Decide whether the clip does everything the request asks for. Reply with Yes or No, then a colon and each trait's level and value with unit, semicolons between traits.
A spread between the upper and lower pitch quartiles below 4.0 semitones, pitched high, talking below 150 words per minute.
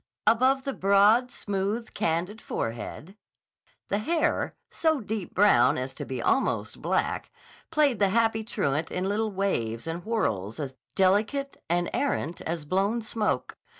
No: wide, 5.4 semitones; high, 200 Hz; average, 140 wpm